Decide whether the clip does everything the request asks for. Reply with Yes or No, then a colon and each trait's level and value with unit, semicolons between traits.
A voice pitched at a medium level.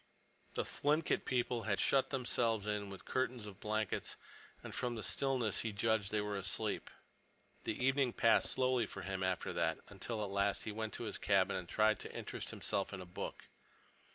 No: low, 110 Hz